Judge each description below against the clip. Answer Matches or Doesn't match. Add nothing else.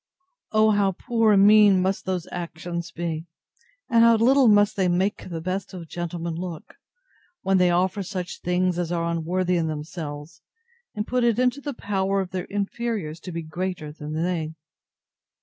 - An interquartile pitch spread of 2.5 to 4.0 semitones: Matches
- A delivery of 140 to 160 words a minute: Doesn't match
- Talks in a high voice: Doesn't match